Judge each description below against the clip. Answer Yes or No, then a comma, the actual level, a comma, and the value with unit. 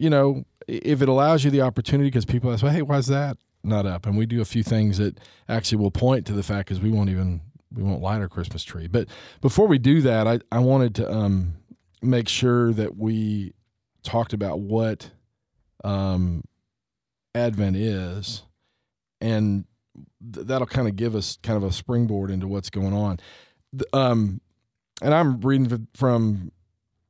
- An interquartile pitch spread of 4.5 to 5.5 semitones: No, average, 3.8 semitones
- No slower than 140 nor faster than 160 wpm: No, average, 180 wpm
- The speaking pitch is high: No, low, 110 Hz